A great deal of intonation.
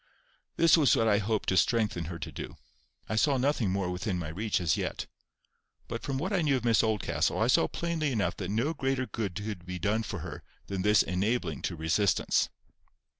Yes: wide, 6.2 semitones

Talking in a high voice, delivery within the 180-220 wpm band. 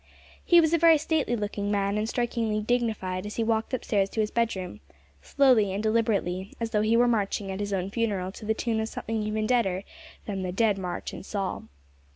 Yes: high, 215 Hz; fast, 205 wpm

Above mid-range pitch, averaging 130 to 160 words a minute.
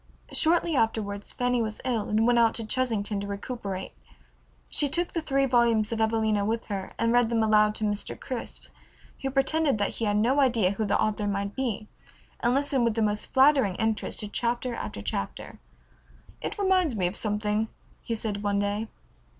No: high, 225 Hz; average, 185 wpm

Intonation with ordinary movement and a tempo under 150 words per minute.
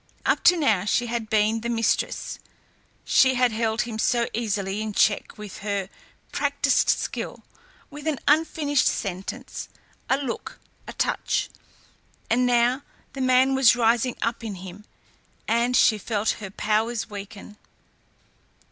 Yes: average, 3.0 semitones; average, 140 wpm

